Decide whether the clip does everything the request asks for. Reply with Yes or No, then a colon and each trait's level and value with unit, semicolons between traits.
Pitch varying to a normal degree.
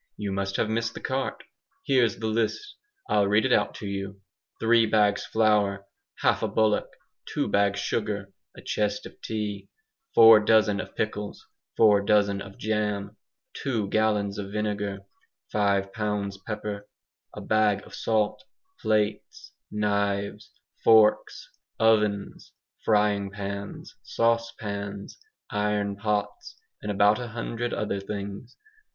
No: narrow, 1.4 semitones